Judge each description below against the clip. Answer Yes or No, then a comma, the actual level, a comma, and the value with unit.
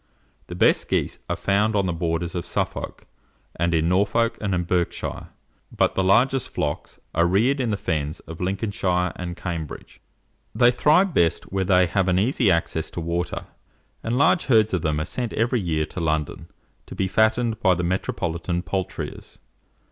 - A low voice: Yes, very low, 90 Hz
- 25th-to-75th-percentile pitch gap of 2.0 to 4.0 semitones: No, average, 4.4 semitones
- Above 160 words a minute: Yes, average, 170 wpm